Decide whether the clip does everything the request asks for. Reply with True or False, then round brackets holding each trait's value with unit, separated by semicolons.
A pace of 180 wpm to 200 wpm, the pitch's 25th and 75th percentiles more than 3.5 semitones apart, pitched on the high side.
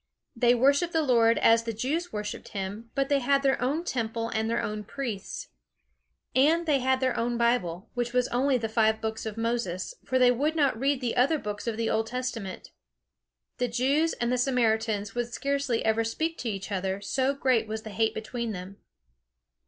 False (195 wpm; 3.2 semitones; 235 Hz)